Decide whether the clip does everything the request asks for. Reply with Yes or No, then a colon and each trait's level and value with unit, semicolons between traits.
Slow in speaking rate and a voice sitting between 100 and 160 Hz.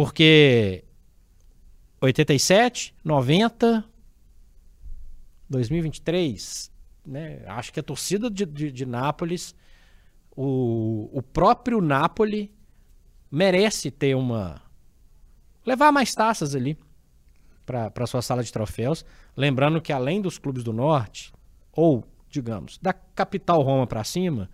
Yes: slow, 110 wpm; low, 135 Hz